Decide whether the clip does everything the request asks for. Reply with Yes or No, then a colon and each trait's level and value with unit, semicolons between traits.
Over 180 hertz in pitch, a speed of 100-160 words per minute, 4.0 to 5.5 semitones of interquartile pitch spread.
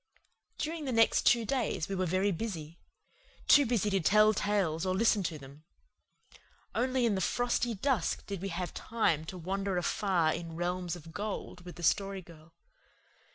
No: high, 190 Hz; average, 170 wpm; average, 4.3 semitones